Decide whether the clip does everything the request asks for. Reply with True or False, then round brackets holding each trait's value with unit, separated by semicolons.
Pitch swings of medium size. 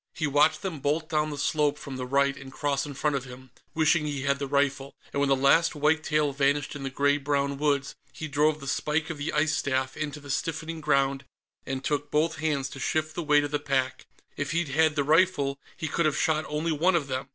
False (1.9 semitones)